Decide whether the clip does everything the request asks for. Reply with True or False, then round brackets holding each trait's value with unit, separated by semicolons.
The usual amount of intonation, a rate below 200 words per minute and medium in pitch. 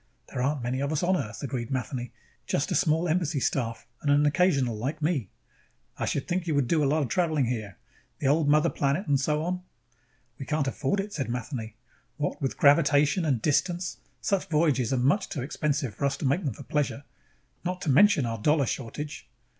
False (3.5 semitones; 205 wpm; 145 Hz)